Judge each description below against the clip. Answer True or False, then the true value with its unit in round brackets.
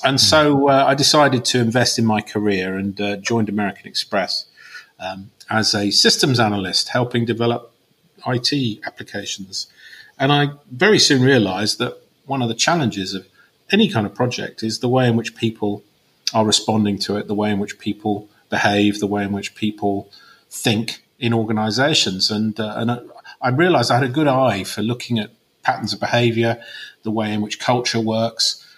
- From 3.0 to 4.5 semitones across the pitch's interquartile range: True (3.3 semitones)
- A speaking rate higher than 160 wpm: True (175 wpm)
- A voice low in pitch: True (115 Hz)